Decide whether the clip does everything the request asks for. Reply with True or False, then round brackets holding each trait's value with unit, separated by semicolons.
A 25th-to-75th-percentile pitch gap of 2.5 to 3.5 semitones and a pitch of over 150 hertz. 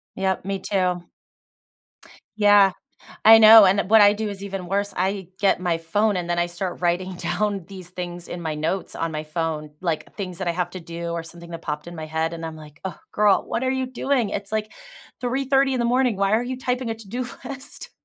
False (4.0 semitones; 190 Hz)